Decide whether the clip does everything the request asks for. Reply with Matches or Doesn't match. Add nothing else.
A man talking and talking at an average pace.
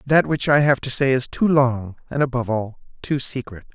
Doesn't match